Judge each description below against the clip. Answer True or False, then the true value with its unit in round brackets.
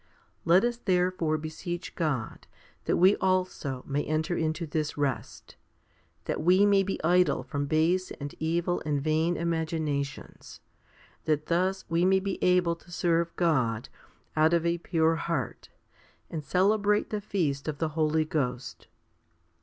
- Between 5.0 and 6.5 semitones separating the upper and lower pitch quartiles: False (2.8 semitones)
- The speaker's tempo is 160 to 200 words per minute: False (145 wpm)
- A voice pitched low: False (165 Hz)